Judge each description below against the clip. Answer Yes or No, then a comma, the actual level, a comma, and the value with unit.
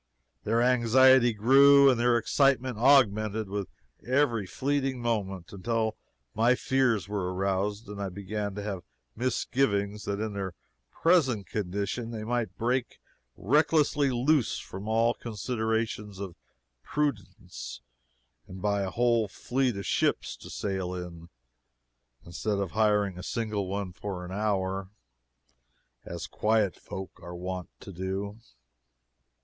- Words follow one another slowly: Yes, slow, 130 wpm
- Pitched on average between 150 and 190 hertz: No, low, 105 Hz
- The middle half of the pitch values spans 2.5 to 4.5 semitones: Yes, average, 3.8 semitones